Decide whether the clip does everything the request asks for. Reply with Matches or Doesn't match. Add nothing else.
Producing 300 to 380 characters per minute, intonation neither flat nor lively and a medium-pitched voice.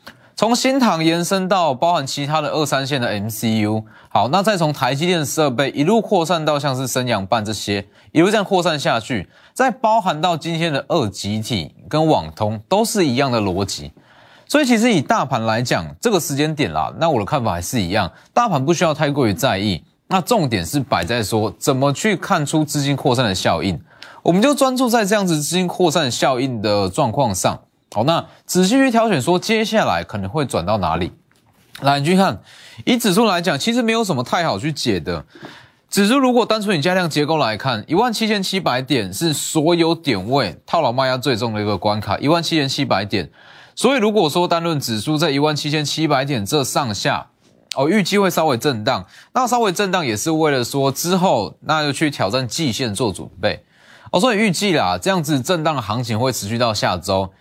Doesn't match